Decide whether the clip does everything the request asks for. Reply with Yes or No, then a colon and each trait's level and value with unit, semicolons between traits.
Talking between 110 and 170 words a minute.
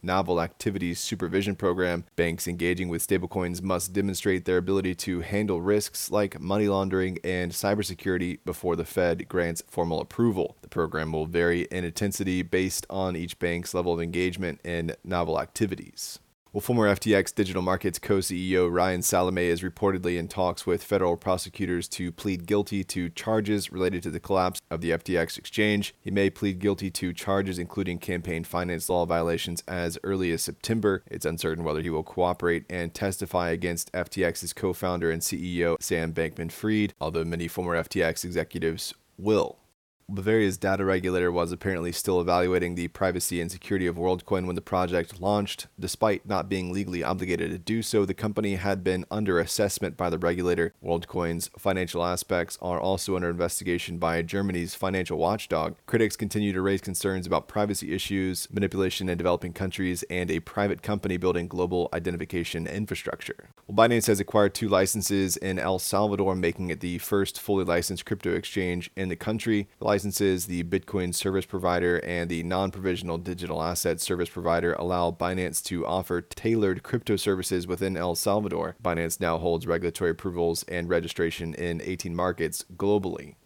Yes: average, 165 wpm